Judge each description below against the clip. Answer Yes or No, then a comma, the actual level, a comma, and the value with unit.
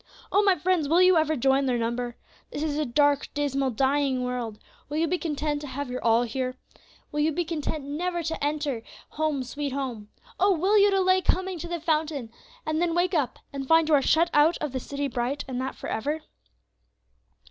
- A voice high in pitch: Yes, very high, 295 Hz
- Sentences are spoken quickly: Yes, fast, 210 wpm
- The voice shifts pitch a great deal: No, average, 3.7 semitones